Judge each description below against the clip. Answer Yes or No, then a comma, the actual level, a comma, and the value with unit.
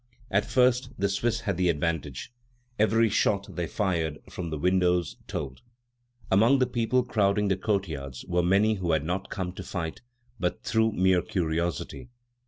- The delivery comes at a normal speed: Yes, average, 160 wpm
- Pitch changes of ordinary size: Yes, average, 4.0 semitones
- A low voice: Yes, very low, 95 Hz